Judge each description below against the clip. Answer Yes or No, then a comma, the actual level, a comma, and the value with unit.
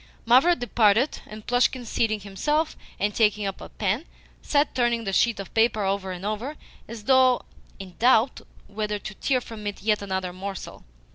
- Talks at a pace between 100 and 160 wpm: No, average, 170 wpm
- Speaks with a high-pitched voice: Yes, high, 215 Hz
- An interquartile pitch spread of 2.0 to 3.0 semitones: No, average, 3.6 semitones